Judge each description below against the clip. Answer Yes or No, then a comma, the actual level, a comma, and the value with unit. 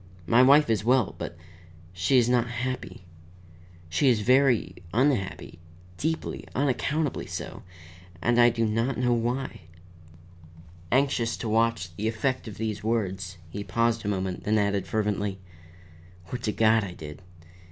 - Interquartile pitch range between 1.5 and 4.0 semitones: Yes, average, 3.7 semitones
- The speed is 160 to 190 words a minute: No, average, 140 wpm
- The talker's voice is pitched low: Yes, low, 115 Hz